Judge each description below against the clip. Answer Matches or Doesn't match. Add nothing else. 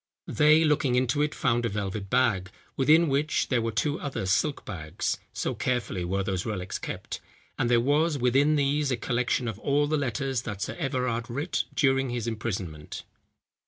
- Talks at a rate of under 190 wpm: Matches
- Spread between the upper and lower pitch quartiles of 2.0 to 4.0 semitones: Doesn't match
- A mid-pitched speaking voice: Doesn't match